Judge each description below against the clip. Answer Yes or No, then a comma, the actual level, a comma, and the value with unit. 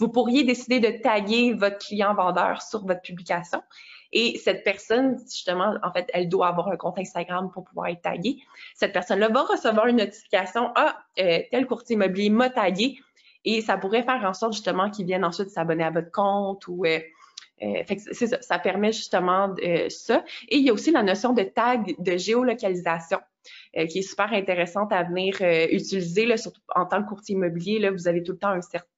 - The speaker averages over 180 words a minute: Yes, average, 205 wpm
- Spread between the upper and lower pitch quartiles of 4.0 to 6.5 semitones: Yes, average, 4.3 semitones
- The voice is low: No, high, 200 Hz